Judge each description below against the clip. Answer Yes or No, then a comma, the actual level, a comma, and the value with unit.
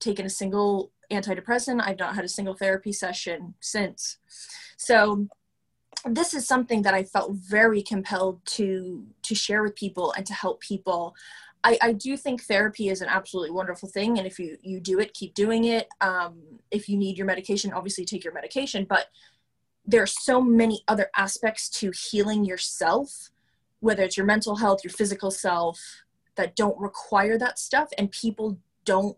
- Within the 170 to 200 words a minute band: Yes, average, 175 wpm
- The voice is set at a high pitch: Yes, high, 200 Hz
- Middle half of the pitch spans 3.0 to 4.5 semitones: No, narrow, 2.5 semitones